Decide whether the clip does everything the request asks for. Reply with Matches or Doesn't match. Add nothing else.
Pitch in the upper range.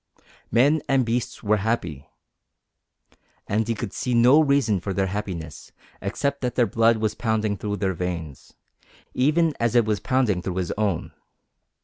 Doesn't match